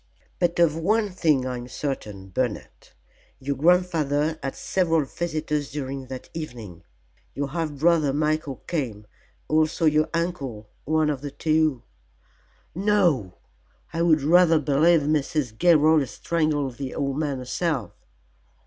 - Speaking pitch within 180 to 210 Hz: No, medium, 150 Hz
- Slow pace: Yes, slow, 130 wpm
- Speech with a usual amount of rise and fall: Yes, average, 3.4 semitones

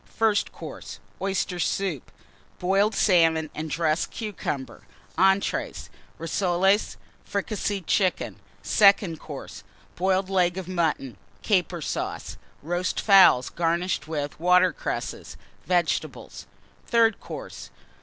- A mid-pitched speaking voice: Yes, medium, 180 Hz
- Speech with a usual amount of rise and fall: Yes, average, 3.1 semitones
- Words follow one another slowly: Yes, slow, 100 wpm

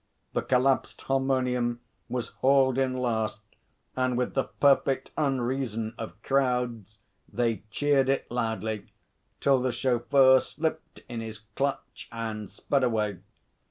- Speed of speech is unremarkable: No, slow, 125 wpm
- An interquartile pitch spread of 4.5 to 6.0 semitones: No, average, 2.8 semitones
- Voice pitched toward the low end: Yes, low, 125 Hz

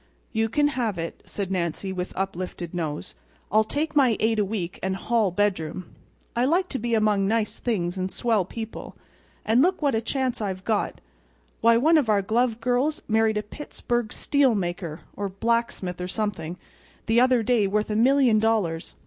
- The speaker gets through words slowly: No, average, 175 wpm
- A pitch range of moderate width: Yes, average, 4.1 semitones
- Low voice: No, high, 220 Hz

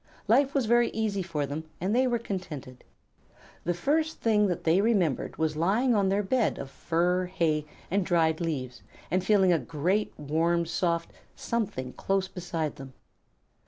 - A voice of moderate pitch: Yes, medium, 180 Hz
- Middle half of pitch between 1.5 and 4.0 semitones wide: No, average, 4.6 semitones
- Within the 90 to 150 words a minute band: No, average, 160 wpm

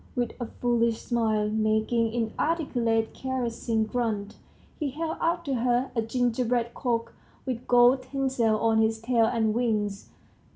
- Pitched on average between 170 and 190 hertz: No, high, 235 Hz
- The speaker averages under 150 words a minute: Yes, slow, 135 wpm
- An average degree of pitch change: No, narrow, 2.1 semitones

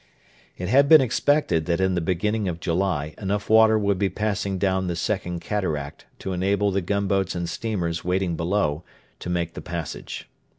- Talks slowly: No, average, 175 wpm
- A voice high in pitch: No, very low, 95 Hz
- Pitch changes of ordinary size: Yes, average, 3.1 semitones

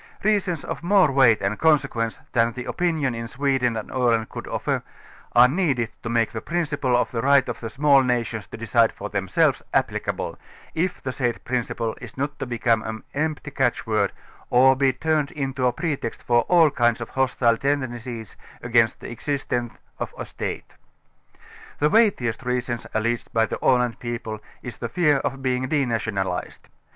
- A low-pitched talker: Yes, low, 125 Hz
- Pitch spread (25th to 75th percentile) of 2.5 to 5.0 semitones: Yes, average, 3.4 semitones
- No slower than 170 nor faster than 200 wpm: Yes, average, 175 wpm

